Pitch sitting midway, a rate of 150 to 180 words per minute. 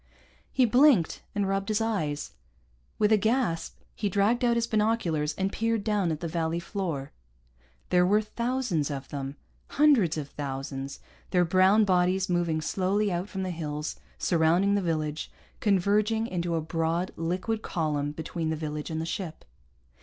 Yes: medium, 180 Hz; average, 160 wpm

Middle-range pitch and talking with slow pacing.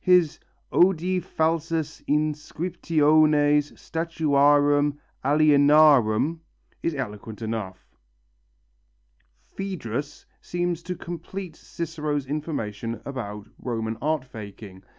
Yes: medium, 150 Hz; slow, 75 wpm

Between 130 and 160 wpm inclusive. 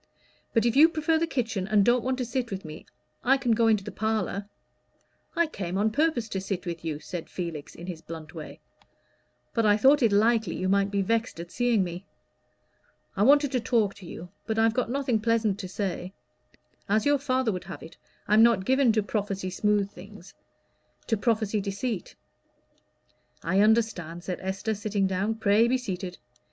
No: average, 190 wpm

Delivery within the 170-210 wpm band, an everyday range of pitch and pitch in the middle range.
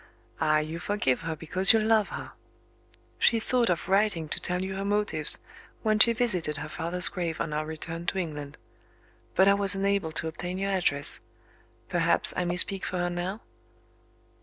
Yes: average, 180 wpm; average, 3.6 semitones; medium, 180 Hz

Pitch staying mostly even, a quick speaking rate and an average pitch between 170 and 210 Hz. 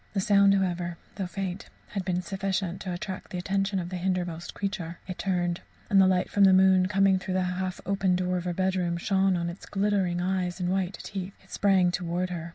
Yes: narrow, 1.5 semitones; fast, 215 wpm; medium, 185 Hz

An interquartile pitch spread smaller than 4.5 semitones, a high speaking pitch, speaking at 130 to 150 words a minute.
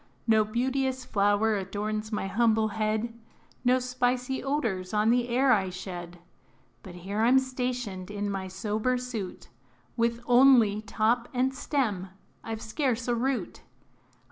Yes: average, 3.4 semitones; high, 225 Hz; average, 140 wpm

